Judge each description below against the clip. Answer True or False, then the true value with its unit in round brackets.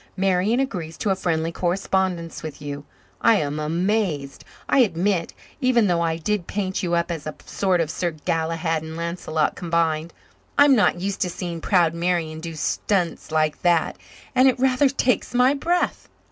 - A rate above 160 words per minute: True (170 wpm)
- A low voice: False (175 Hz)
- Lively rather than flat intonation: False (3.9 semitones)